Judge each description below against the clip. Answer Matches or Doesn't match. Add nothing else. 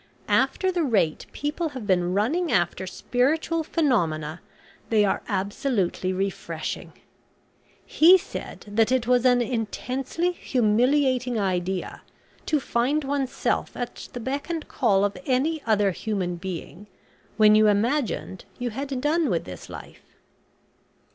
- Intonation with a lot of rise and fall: Matches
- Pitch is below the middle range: Doesn't match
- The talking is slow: Matches